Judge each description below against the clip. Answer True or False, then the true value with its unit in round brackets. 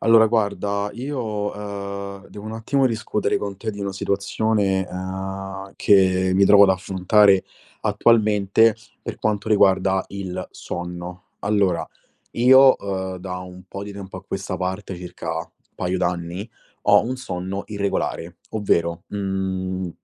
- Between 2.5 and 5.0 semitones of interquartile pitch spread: False (1.9 semitones)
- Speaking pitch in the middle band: False (100 Hz)